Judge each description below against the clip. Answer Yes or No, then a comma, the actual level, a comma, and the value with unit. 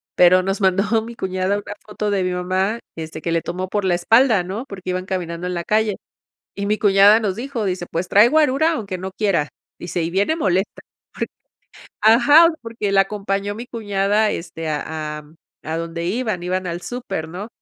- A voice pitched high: Yes, high, 195 Hz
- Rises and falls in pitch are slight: No, average, 3.2 semitones